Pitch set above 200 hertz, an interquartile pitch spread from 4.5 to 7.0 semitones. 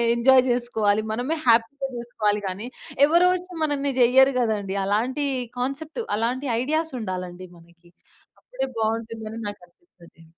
Yes: high, 235 Hz; average, 4.9 semitones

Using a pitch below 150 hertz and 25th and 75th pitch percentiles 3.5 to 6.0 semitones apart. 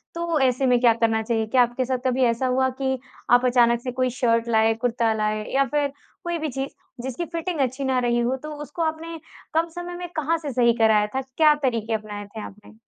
No: very high, 255 Hz; average, 4.0 semitones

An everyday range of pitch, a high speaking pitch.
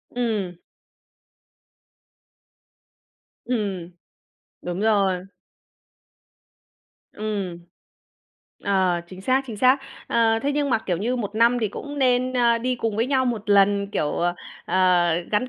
Yes: average, 4.6 semitones; high, 215 Hz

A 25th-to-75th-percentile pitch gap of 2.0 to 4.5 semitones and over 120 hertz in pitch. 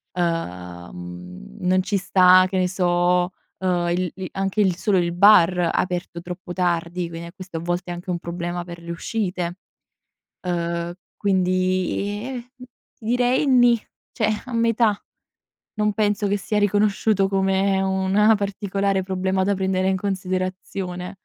Yes: narrow, 2.3 semitones; medium, 185 Hz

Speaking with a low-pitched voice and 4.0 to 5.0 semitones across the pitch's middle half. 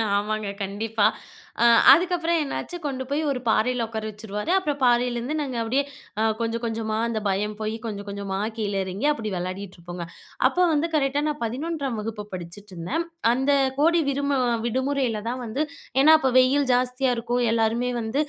No: high, 240 Hz; average, 4.7 semitones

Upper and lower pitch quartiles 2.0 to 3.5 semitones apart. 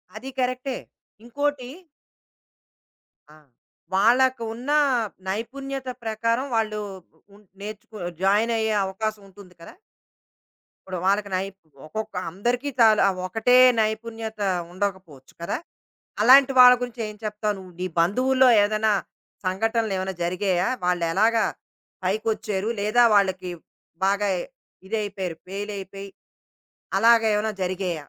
Yes: average, 3.2 semitones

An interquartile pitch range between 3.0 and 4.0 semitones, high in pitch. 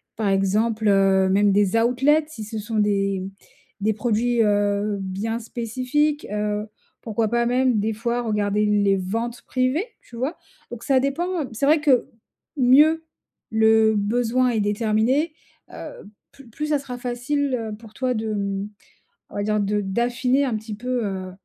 Yes: average, 3.5 semitones; high, 225 Hz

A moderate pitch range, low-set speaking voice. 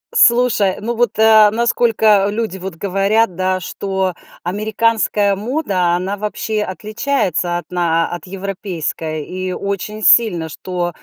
No: average, 3.2 semitones; high, 200 Hz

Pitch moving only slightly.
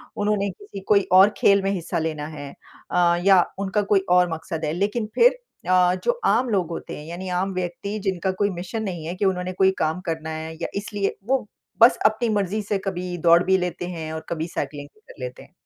No: average, 3.2 semitones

